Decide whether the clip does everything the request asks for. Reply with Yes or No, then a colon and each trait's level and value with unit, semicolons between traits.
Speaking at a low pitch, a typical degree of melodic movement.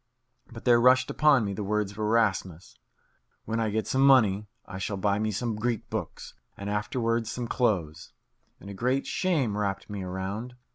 Yes: low, 110 Hz; average, 3.3 semitones